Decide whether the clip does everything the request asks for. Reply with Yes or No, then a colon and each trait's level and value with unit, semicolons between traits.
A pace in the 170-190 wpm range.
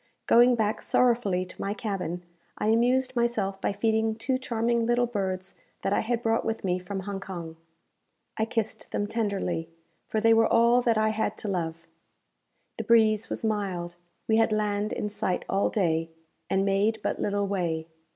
Yes: average, 175 wpm